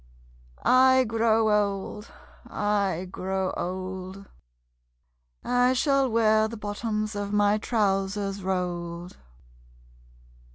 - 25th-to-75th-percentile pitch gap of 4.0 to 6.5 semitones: No, average, 2.7 semitones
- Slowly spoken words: Yes, slow, 85 wpm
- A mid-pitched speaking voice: No, high, 205 Hz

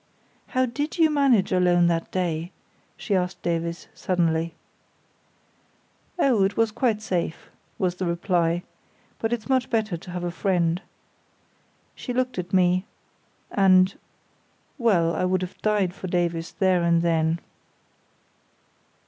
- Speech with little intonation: No, average, 3.8 semitones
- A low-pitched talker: No, medium, 185 Hz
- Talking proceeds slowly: Yes, slow, 130 wpm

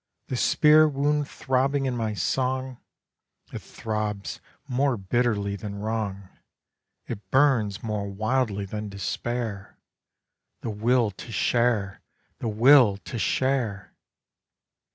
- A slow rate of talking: Yes, slow, 110 wpm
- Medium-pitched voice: No, low, 115 Hz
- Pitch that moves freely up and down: No, average, 4.3 semitones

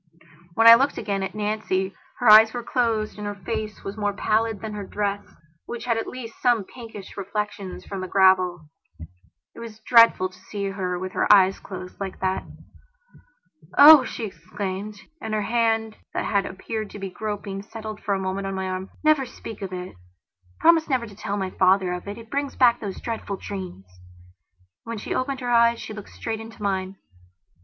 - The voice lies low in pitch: No, high, 205 Hz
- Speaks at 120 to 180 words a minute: No, average, 195 wpm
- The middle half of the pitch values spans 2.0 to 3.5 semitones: Yes, average, 3.1 semitones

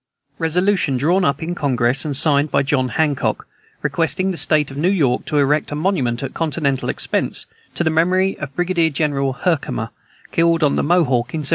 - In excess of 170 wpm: Yes, average, 185 wpm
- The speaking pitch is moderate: Yes, medium, 150 Hz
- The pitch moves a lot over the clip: No, average, 3.6 semitones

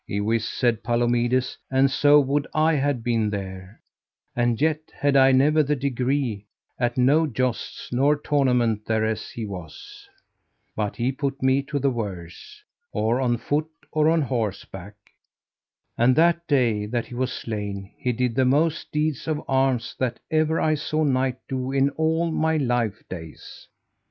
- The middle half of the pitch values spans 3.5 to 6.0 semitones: Yes, average, 4.0 semitones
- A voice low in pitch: Yes, low, 130 Hz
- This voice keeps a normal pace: Yes, average, 155 wpm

